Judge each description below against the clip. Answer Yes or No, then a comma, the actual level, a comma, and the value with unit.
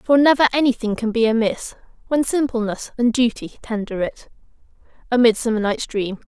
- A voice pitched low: No, high, 245 Hz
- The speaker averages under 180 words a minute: Yes, average, 150 wpm